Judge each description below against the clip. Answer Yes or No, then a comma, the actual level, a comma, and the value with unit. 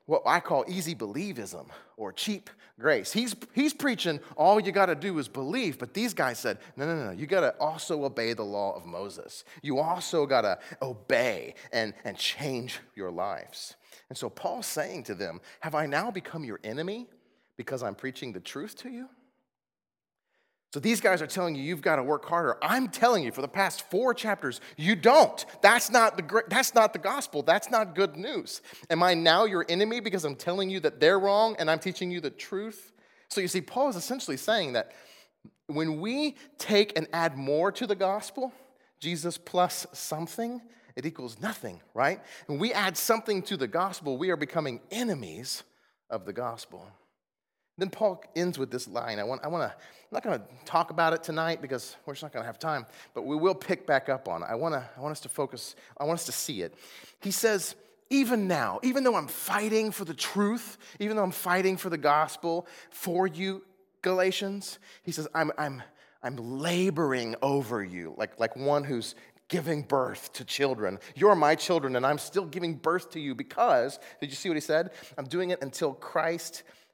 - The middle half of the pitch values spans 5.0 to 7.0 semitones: Yes, wide, 5.5 semitones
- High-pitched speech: No, medium, 180 Hz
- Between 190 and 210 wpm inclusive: Yes, average, 200 wpm